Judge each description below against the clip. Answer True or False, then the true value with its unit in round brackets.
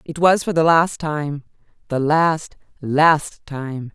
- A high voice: False (150 Hz)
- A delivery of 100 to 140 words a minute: True (135 wpm)